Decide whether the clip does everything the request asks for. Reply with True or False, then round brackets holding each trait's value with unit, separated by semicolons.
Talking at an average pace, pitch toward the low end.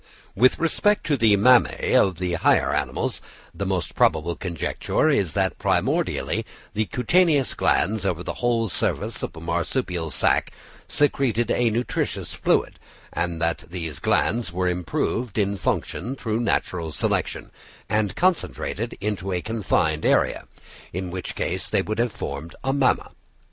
True (145 wpm; 100 Hz)